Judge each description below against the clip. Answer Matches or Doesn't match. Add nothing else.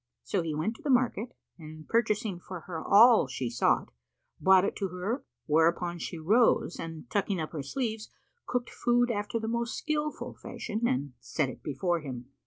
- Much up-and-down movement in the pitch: Matches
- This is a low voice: Doesn't match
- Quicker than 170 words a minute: Matches